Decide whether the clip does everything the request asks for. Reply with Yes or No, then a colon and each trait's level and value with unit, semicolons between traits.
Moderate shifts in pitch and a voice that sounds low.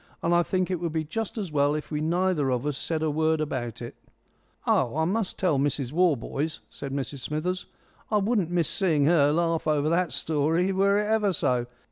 No: average, 3.9 semitones; medium, 160 Hz